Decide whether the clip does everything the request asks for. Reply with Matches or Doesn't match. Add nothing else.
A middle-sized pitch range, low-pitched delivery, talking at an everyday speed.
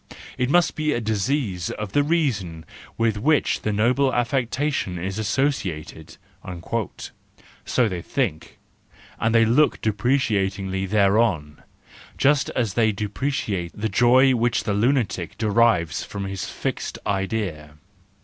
Doesn't match